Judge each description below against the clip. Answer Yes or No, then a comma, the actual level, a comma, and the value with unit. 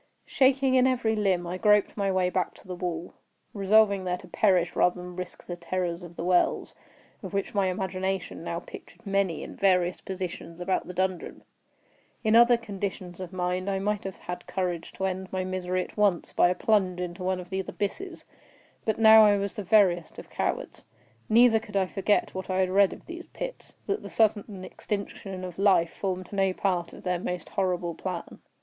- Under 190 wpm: No, average, 195 wpm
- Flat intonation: Yes, narrow, 2.3 semitones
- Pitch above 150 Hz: Yes, high, 190 Hz